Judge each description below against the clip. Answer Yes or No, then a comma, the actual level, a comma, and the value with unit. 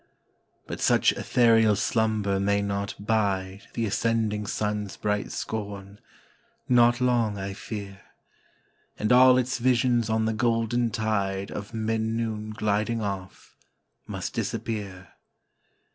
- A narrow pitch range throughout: Yes, narrow, 2.2 semitones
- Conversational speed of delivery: No, slow, 115 wpm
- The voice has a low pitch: Yes, low, 110 Hz